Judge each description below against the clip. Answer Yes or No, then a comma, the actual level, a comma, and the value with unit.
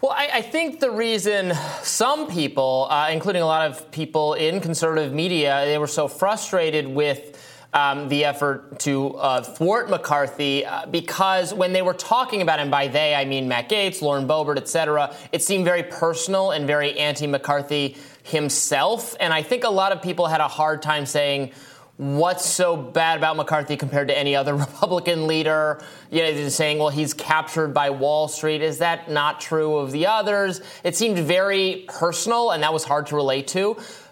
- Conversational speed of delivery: Yes, average, 190 wpm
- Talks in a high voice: No, medium, 155 Hz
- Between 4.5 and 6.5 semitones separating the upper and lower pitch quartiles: No, average, 3.6 semitones